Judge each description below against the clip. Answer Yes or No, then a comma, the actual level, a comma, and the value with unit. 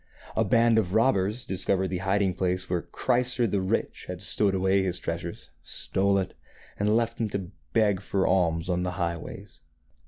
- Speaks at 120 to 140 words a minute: No, average, 175 wpm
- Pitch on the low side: Yes, very low, 95 Hz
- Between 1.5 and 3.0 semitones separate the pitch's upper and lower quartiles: Yes, average, 2.7 semitones